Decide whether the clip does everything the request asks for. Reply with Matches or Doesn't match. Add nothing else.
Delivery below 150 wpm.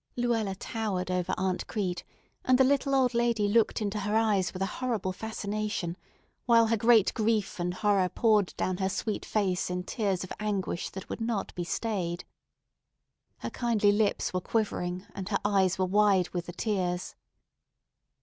Doesn't match